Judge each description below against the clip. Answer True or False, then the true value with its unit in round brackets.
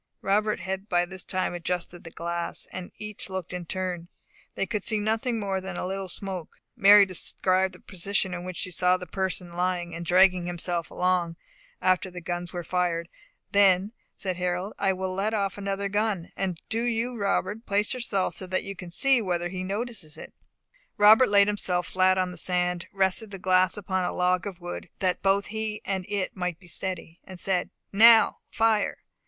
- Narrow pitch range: True (2.1 semitones)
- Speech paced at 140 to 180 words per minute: False (190 wpm)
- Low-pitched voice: False (185 Hz)